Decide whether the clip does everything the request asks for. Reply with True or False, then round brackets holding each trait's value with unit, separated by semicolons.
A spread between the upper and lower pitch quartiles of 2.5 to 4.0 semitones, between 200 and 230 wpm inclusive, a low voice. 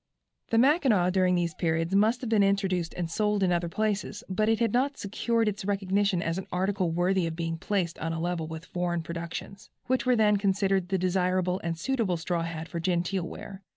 False (3.2 semitones; 205 wpm; 185 Hz)